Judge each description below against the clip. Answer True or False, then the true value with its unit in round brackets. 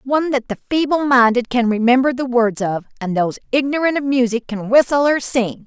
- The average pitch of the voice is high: True (250 Hz)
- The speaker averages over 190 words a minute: True (200 wpm)